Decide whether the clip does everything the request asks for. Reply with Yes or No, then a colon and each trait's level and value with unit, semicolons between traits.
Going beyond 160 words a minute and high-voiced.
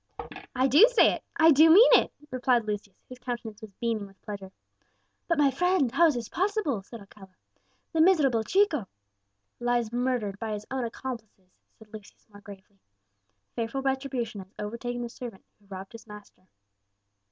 Yes: average, 170 wpm; high, 235 Hz